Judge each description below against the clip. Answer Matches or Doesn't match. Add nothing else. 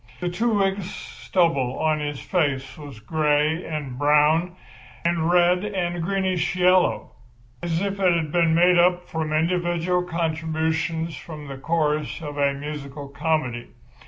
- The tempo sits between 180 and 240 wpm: Doesn't match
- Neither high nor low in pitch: Matches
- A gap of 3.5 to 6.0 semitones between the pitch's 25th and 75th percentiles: Doesn't match